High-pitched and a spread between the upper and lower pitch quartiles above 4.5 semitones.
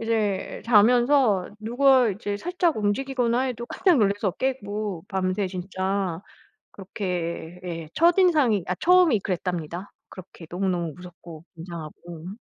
Yes: high, 200 Hz; average, 5.3 semitones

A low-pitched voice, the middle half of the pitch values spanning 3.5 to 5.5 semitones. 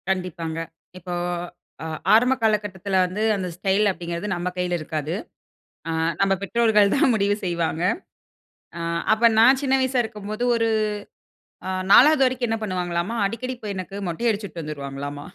No: high, 195 Hz; average, 4.5 semitones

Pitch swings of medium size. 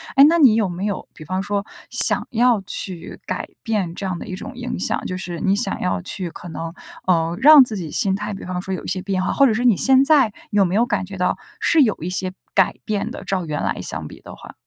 Yes: average, 3.7 semitones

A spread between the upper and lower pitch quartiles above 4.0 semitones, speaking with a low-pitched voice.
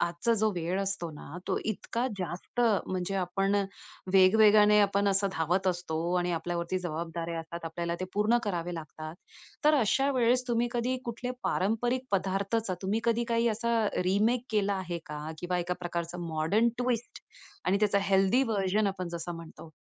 No: average, 4.4 semitones; high, 195 Hz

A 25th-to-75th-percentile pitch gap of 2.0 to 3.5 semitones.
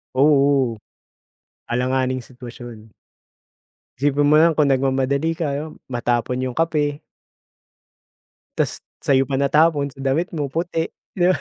Yes: average, 2.8 semitones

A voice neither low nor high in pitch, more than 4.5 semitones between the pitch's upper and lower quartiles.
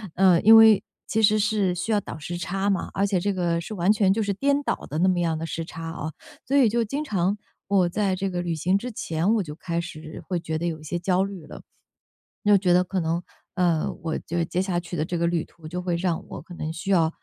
No: medium, 180 Hz; average, 3.1 semitones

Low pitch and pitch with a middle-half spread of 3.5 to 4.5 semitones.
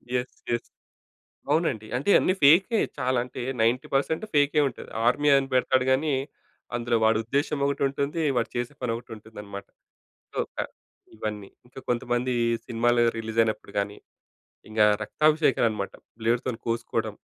Yes: low, 120 Hz; average, 3.9 semitones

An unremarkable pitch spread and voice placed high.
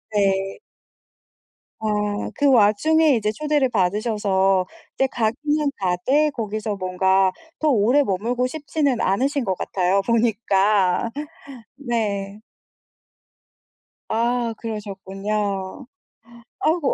Yes: average, 4.6 semitones; high, 215 Hz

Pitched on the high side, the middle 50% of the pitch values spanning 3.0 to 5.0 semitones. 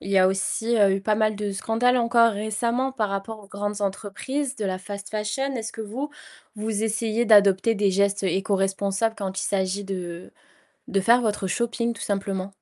No: high, 205 Hz; narrow, 2.6 semitones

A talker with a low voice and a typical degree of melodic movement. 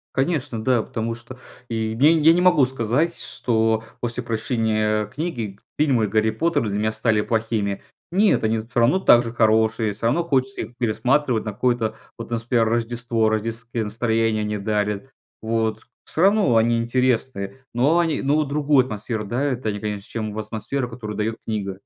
Yes: low, 115 Hz; average, 3.0 semitones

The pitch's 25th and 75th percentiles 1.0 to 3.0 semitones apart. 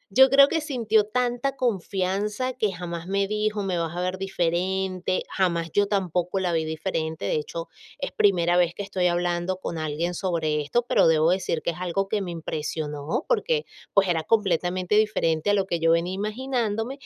No: average, 3.8 semitones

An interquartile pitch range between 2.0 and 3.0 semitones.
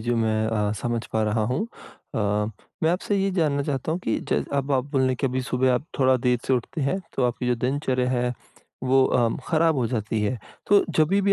No: average, 3.6 semitones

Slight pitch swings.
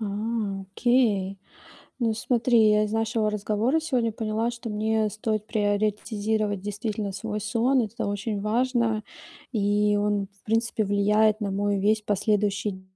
Yes: narrow, 1.7 semitones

